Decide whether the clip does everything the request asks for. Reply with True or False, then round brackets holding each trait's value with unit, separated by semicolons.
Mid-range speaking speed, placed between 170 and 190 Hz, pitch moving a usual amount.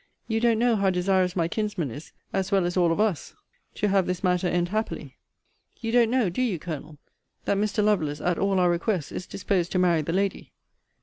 False (210 wpm; 185 Hz; 3.3 semitones)